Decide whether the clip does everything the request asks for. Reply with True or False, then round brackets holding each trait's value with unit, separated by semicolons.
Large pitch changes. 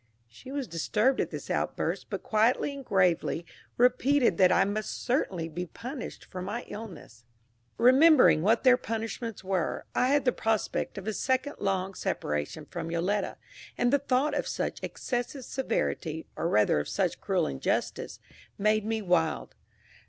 True (6.1 semitones)